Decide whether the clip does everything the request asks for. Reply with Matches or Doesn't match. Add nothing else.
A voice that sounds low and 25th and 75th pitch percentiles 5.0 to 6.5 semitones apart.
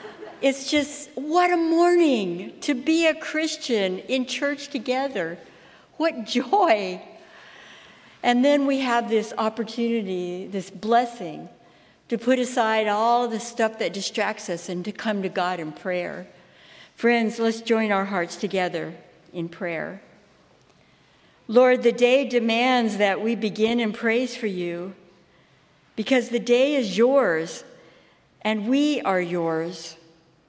Doesn't match